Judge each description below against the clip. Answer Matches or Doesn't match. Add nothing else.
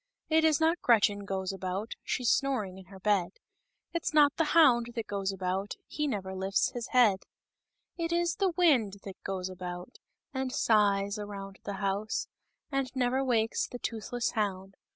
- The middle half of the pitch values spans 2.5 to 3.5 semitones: Doesn't match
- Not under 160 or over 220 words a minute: Matches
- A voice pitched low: Doesn't match